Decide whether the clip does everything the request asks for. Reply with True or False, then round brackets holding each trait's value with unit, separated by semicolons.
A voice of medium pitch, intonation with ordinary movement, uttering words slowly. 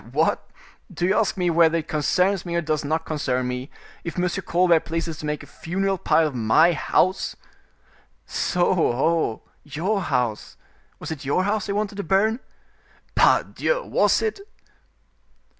False (170 Hz; 4.0 semitones; 155 wpm)